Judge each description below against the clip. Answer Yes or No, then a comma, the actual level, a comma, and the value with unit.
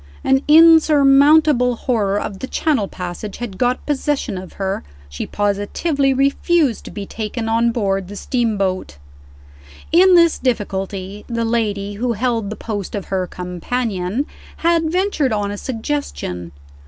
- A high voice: Yes, high, 230 Hz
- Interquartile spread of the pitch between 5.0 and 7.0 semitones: Yes, wide, 5.6 semitones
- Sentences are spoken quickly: No, average, 140 wpm